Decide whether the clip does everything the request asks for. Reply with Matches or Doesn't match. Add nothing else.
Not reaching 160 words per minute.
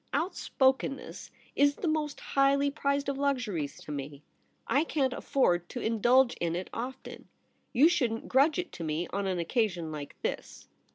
Doesn't match